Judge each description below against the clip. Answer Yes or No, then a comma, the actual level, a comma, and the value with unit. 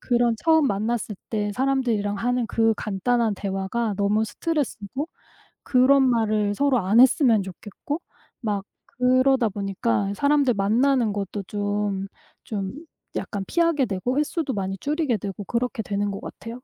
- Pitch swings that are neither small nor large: Yes, average, 4.3 semitones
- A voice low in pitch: No, high, 225 Hz